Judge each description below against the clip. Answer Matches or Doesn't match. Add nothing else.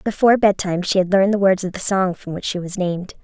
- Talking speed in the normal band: Doesn't match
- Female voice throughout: Matches